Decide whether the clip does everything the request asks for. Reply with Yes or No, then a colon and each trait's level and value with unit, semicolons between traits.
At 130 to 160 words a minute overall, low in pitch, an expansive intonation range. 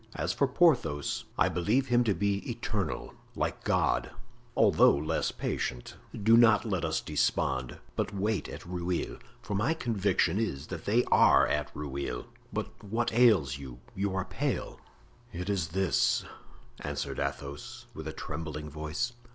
Yes: average, 150 wpm; very low, 95 Hz; wide, 6.7 semitones